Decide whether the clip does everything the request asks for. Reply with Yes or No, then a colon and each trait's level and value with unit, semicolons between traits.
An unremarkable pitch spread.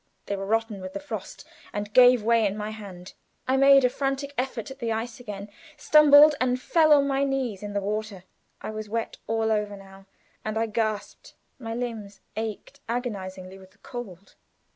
Yes: average, 3.8 semitones